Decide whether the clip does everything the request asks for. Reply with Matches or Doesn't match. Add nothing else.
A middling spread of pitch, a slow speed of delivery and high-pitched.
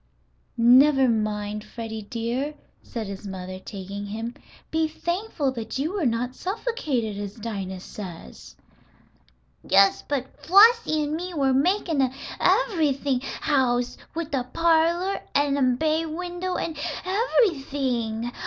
Doesn't match